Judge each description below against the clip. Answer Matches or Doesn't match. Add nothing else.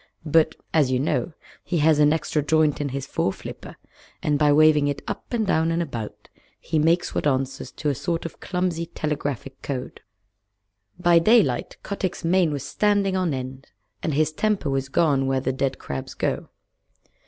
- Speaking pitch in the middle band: Matches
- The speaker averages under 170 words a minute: Doesn't match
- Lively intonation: Doesn't match